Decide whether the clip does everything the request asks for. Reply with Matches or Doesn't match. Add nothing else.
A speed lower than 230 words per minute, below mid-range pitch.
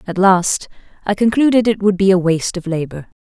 Doesn't match